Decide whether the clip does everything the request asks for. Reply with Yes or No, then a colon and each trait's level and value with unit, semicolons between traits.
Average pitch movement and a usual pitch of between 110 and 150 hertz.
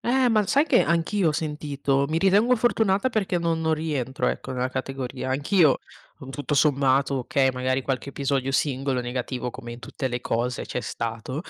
Yes: average, 4.3 semitones; medium, 140 Hz